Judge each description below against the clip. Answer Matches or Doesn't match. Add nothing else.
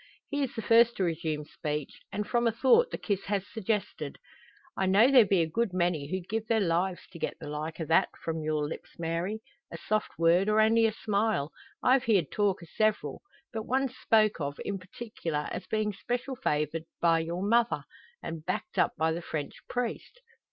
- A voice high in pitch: Matches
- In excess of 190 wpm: Matches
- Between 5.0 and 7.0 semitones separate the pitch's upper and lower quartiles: Matches